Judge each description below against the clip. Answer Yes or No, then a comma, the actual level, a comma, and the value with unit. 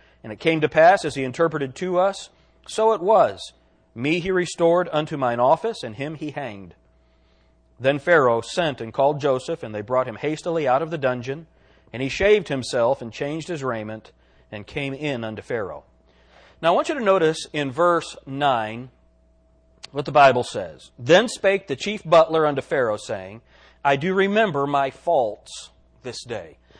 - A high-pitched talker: No, medium, 140 Hz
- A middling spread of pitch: No, wide, 6.7 semitones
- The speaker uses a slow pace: No, average, 175 wpm